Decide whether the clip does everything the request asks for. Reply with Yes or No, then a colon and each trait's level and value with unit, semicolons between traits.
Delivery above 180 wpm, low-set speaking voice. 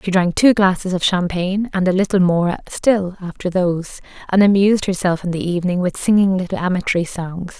No: average, 190 wpm; medium, 185 Hz